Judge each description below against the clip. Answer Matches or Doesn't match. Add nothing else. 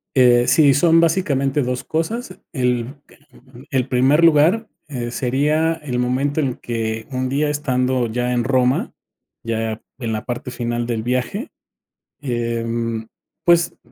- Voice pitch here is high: Doesn't match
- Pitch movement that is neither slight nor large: Matches